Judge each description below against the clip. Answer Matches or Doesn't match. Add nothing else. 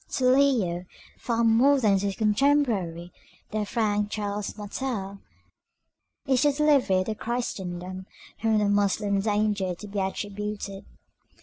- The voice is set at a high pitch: Matches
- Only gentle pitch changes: Doesn't match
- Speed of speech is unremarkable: Doesn't match